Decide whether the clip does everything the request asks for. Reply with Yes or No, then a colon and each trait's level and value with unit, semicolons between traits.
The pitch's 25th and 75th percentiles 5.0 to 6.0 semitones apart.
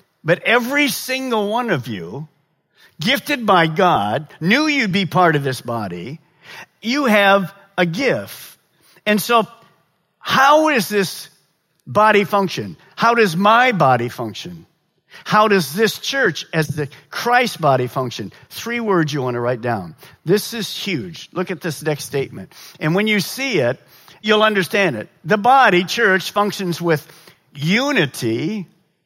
Yes: wide, 5.4 semitones